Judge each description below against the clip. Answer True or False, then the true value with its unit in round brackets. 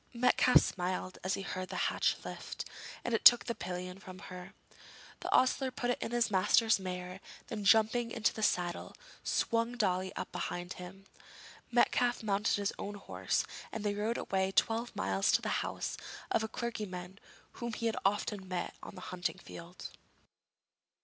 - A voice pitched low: False (200 Hz)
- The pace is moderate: True (165 wpm)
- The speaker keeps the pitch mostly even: False (4.0 semitones)